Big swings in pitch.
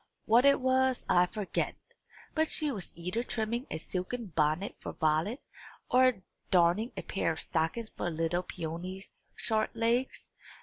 Yes: wide, 6.0 semitones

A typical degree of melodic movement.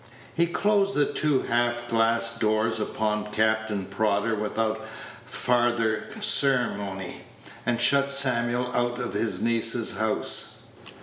No: narrow, 2.2 semitones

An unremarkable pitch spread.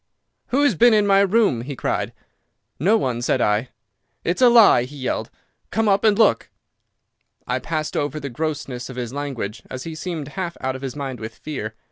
No: wide, 7.6 semitones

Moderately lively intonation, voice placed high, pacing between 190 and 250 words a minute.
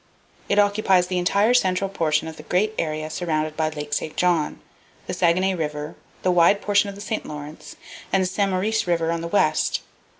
No: average, 4.1 semitones; medium, 180 Hz; average, 195 wpm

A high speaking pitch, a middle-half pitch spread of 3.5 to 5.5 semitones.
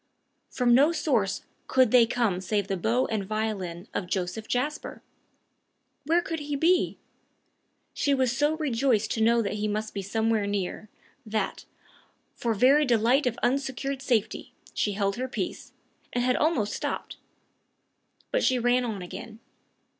Yes: high, 235 Hz; average, 4.1 semitones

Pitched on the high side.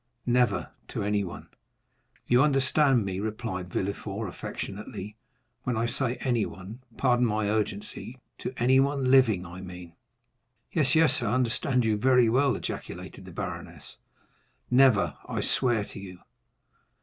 No: low, 120 Hz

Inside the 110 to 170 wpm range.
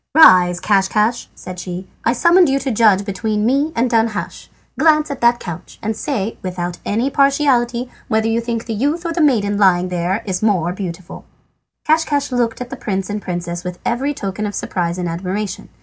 No: average, 185 wpm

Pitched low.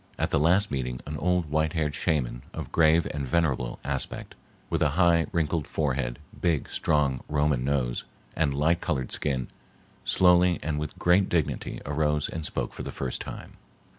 Yes: very low, 75 Hz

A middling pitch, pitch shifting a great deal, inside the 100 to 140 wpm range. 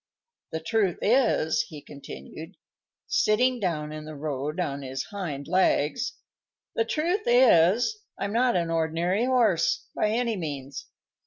Yes: medium, 180 Hz; wide, 7.0 semitones; slow, 135 wpm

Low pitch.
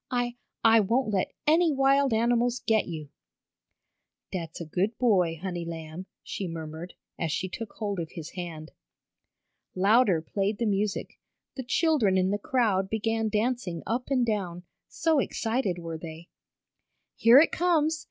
No: high, 205 Hz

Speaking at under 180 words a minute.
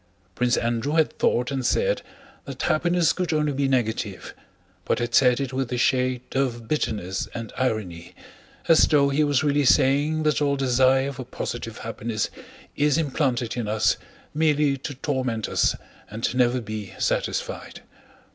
Yes: average, 155 wpm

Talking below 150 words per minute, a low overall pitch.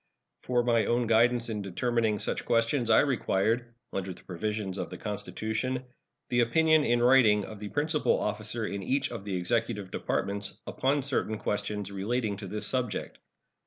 No: average, 160 wpm; low, 110 Hz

